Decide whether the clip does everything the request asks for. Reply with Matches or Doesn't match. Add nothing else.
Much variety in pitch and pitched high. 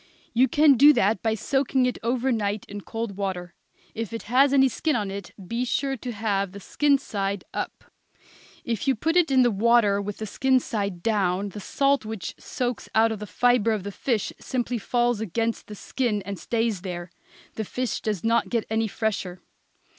Doesn't match